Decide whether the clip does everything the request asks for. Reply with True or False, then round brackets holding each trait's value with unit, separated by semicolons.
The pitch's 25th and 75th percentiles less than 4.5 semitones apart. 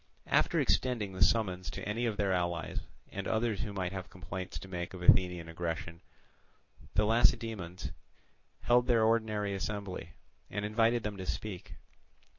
True (3.6 semitones)